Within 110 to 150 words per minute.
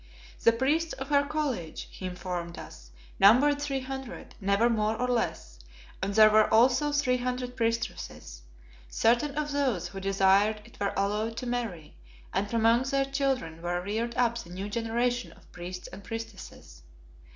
No: average, 160 wpm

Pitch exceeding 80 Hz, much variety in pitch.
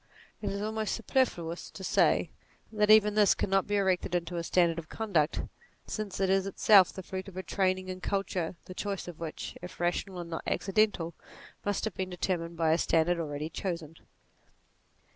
No: medium, 185 Hz; average, 2.8 semitones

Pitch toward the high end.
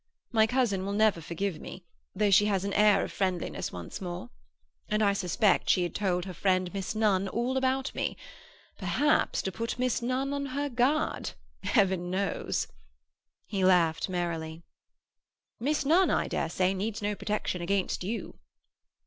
Yes: high, 200 Hz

